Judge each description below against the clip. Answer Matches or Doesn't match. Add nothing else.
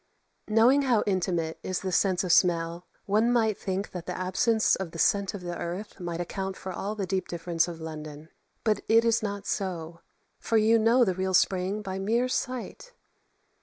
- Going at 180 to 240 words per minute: Matches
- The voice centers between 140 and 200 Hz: Matches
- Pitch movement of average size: Matches